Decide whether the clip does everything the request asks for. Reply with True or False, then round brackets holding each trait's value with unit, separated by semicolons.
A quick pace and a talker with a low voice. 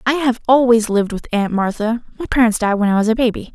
False (235 wpm; 230 Hz)